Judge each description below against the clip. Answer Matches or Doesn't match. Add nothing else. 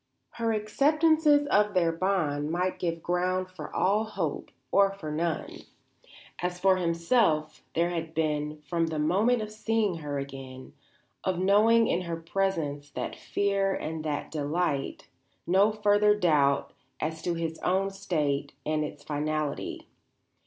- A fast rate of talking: Doesn't match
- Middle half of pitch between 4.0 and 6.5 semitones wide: Matches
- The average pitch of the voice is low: Doesn't match